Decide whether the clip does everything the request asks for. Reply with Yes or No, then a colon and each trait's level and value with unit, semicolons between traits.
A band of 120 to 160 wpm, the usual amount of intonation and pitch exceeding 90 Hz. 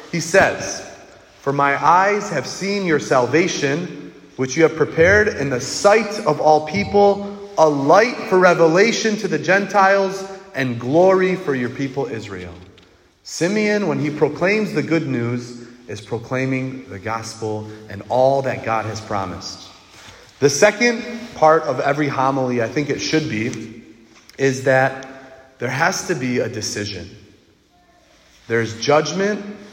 No: average, 140 wpm; wide, 8.0 semitones; medium, 140 Hz